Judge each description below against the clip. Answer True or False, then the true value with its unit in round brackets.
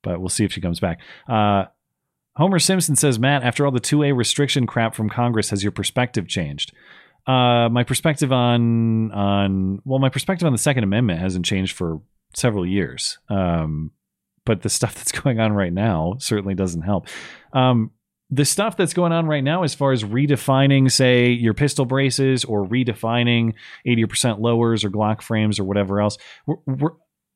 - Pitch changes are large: False (5.0 semitones)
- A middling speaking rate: True (180 wpm)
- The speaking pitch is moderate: False (120 Hz)